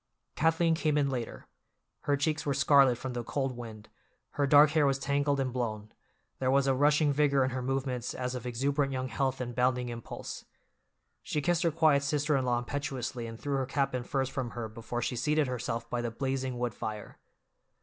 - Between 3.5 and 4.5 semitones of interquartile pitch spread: No, narrow, 2.6 semitones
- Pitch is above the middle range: No, low, 135 Hz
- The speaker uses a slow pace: No, average, 200 wpm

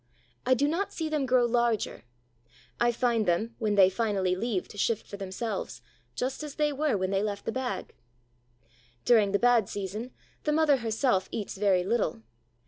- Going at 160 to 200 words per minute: Yes, average, 175 wpm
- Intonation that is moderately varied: Yes, average, 4.3 semitones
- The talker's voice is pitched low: No, high, 225 Hz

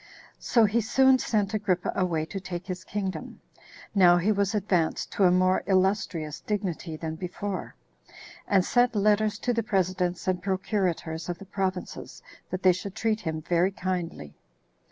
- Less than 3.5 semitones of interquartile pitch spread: Yes, narrow, 2.6 semitones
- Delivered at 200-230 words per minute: No, average, 155 wpm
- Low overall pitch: No, medium, 185 Hz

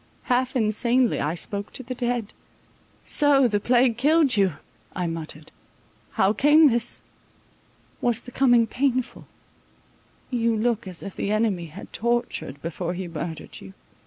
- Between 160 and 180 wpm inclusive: No, average, 140 wpm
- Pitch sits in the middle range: No, high, 230 Hz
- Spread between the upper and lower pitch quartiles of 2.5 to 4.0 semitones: No, average, 4.9 semitones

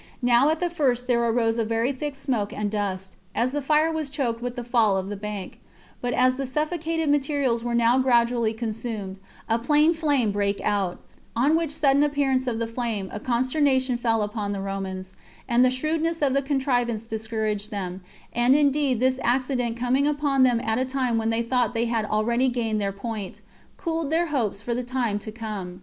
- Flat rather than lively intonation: No, average, 3.8 semitones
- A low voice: No, high, 240 Hz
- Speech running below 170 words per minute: No, average, 200 wpm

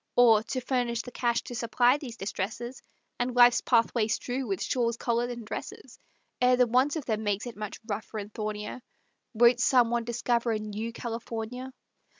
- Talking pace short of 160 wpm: No, average, 175 wpm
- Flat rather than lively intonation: Yes, narrow, 2.0 semitones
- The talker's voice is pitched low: No, high, 235 Hz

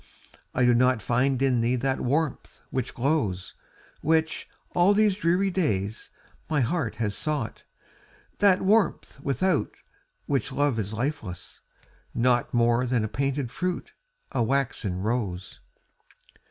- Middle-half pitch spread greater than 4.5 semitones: Yes, average, 5.1 semitones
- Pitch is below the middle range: Yes, low, 130 Hz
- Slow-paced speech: Yes, slow, 125 wpm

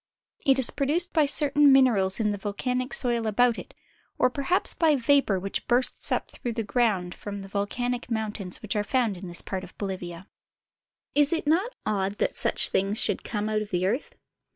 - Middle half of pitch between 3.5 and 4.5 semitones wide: No, average, 5.0 semitones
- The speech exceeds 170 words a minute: Yes, average, 200 wpm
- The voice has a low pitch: No, high, 225 Hz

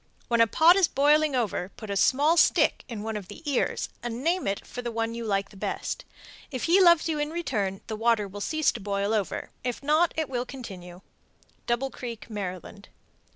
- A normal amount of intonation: No, wide, 6.4 semitones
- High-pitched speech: Yes, high, 235 Hz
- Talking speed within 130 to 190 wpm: No, average, 200 wpm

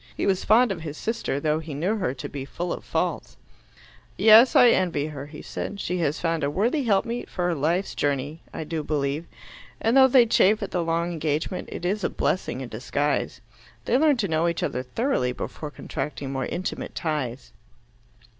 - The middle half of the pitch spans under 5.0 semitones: No, wide, 5.6 semitones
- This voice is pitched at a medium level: Yes, medium, 165 Hz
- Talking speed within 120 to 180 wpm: No, average, 190 wpm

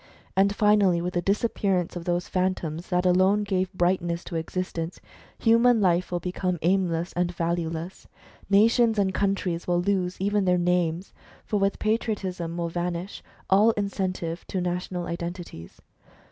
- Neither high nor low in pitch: Yes, medium, 180 Hz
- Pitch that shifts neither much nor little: No, narrow, 2.2 semitones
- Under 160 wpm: Yes, average, 145 wpm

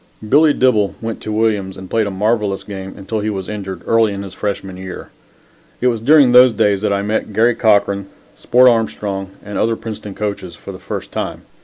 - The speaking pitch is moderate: No, low, 105 Hz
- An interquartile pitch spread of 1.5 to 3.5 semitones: Yes, narrow, 2.6 semitones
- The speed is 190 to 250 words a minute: Yes, average, 200 wpm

